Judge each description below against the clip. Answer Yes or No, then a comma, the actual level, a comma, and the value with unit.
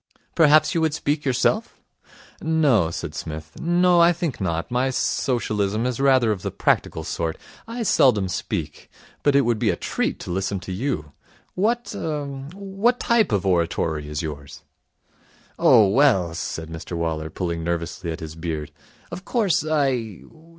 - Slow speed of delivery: No, average, 155 wpm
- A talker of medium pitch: No, low, 115 Hz